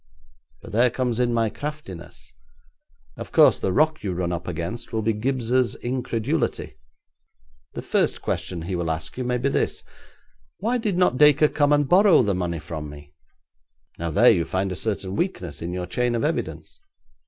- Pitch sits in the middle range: No, low, 115 Hz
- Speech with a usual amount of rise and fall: No, wide, 7.4 semitones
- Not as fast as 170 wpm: No, average, 175 wpm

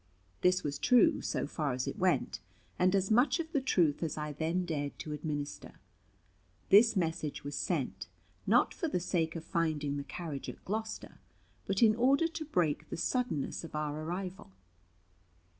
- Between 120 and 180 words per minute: Yes, average, 170 wpm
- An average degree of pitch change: No, wide, 6.3 semitones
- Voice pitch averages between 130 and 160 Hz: No, medium, 170 Hz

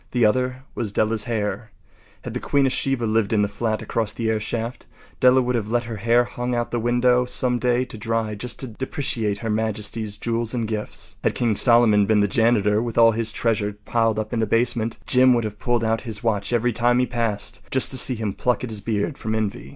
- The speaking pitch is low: Yes, low, 115 Hz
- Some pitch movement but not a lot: No, narrow, 2.1 semitones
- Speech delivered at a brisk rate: Yes, fast, 230 wpm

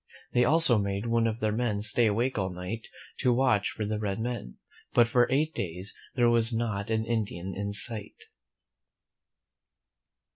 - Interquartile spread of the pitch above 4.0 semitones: No, average, 2.8 semitones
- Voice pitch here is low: Yes, low, 110 Hz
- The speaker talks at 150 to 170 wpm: Yes, average, 160 wpm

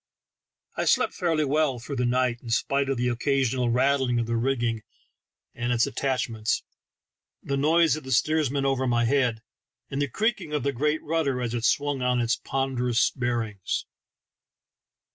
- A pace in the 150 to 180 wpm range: Yes, average, 160 wpm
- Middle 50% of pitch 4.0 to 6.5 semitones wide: No, average, 2.7 semitones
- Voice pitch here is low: Yes, low, 130 Hz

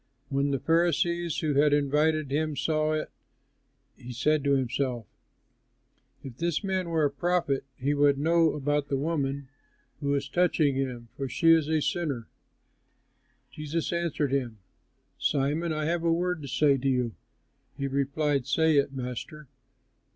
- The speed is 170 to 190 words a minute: No, average, 150 wpm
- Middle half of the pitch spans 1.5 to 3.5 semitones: Yes, average, 2.7 semitones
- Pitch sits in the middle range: Yes, medium, 145 Hz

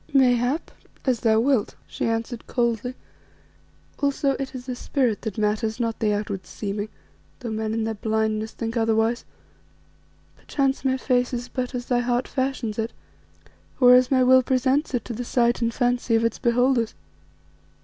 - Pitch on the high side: Yes, high, 240 Hz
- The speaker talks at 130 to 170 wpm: Yes, average, 165 wpm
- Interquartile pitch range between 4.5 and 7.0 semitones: No, narrow, 2.4 semitones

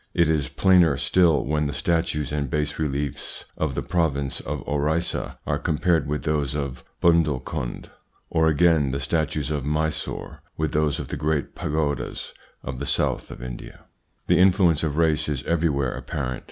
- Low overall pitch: Yes, very low, 75 Hz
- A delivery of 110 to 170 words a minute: Yes, average, 165 wpm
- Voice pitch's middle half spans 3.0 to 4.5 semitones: No, narrow, 2.4 semitones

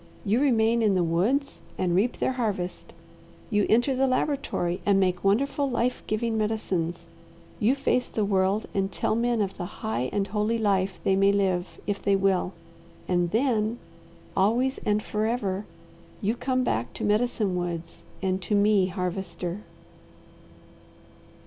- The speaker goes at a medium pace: Yes, average, 150 wpm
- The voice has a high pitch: Yes, high, 205 Hz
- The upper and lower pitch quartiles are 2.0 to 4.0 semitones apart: Yes, average, 3.7 semitones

